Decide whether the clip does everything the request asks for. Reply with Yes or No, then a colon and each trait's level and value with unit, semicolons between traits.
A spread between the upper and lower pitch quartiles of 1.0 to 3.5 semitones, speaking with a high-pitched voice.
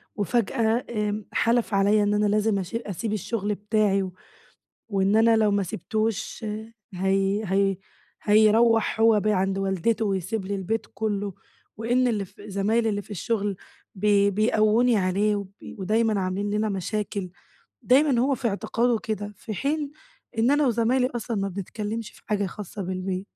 Yes: narrow, 2.4 semitones; high, 210 Hz